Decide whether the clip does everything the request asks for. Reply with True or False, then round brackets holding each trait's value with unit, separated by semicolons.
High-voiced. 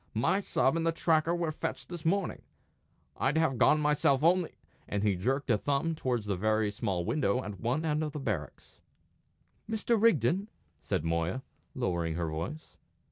False (135 Hz)